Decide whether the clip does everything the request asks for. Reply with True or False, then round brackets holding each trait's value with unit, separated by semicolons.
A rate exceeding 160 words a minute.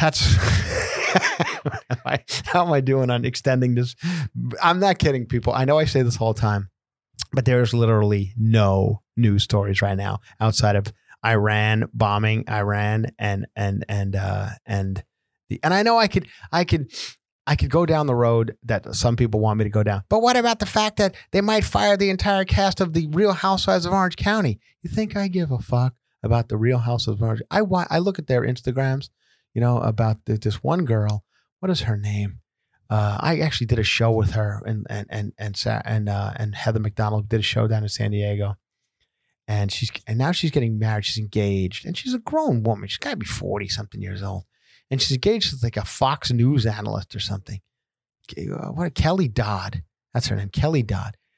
True (205 wpm)